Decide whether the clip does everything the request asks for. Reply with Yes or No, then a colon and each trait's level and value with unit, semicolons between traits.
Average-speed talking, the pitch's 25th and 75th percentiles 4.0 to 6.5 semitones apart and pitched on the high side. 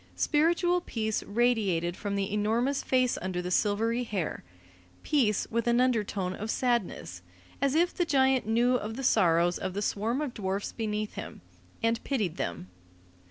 Yes: average, 160 wpm; average, 4.4 semitones; high, 220 Hz